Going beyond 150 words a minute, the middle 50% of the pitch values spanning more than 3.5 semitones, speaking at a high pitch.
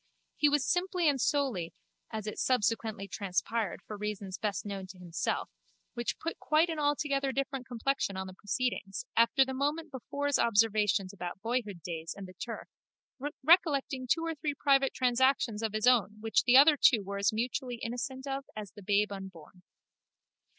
Yes: average, 170 wpm; average, 5.3 semitones; high, 235 Hz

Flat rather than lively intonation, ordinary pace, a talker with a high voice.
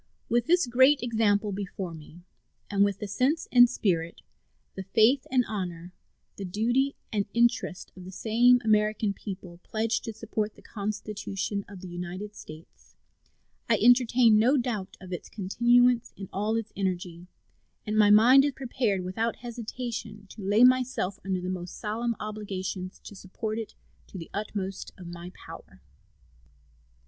No: average, 3.9 semitones; average, 150 wpm; high, 210 Hz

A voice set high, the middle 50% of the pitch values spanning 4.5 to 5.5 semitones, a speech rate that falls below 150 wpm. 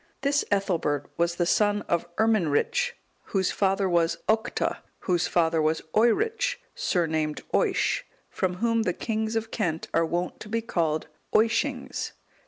Yes: high, 195 Hz; average, 5.1 semitones; average, 140 wpm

